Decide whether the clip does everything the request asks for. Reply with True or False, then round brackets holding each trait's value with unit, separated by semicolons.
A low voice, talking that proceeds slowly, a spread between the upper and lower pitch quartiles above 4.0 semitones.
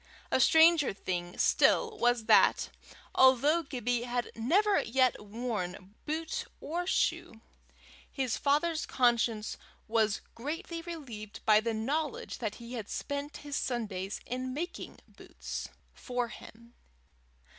False (245 Hz; 115 wpm; 5.1 semitones)